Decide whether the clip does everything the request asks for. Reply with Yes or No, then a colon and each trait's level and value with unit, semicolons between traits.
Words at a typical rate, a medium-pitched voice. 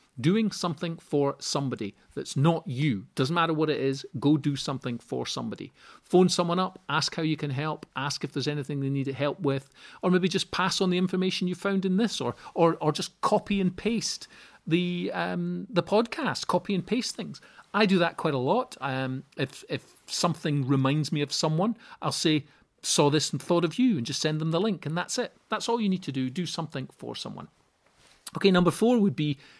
No: fast, 215 wpm; medium, 165 Hz